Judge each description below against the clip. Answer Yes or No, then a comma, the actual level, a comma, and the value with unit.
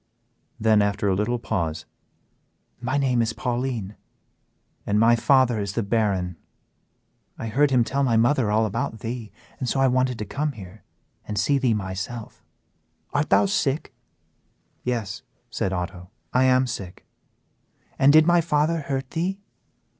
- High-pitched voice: No, low, 120 Hz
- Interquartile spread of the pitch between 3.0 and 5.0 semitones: Yes, average, 4.4 semitones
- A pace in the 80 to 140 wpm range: No, average, 150 wpm